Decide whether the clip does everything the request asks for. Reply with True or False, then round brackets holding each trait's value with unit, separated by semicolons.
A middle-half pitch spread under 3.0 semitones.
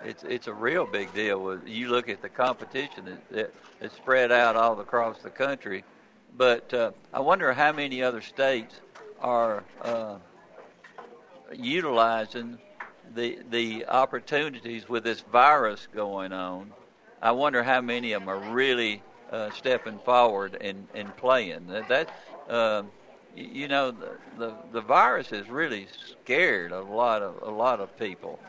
True (2.4 semitones)